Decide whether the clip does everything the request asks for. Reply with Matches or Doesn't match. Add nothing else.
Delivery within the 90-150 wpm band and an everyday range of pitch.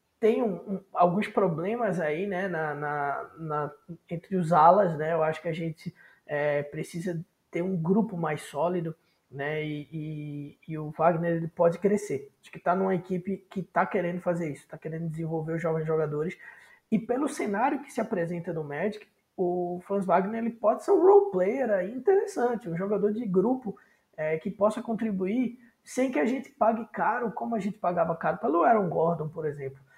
Doesn't match